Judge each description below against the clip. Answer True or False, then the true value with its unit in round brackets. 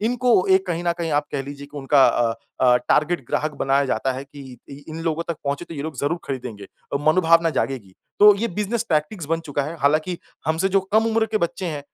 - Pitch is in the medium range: True (155 Hz)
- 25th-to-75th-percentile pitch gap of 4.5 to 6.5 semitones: False (4.1 semitones)